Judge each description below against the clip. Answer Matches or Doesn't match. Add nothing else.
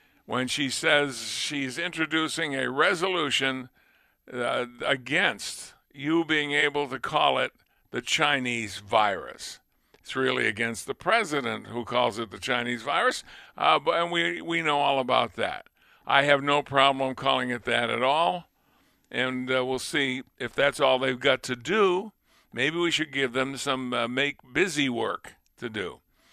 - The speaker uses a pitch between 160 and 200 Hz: Doesn't match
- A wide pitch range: Doesn't match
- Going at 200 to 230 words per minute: Doesn't match